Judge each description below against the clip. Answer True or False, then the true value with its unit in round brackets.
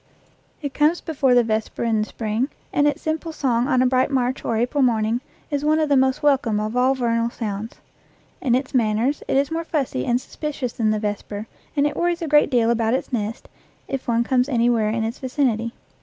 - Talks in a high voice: True (250 Hz)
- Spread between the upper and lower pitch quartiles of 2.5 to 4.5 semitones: True (3.9 semitones)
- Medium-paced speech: False (215 wpm)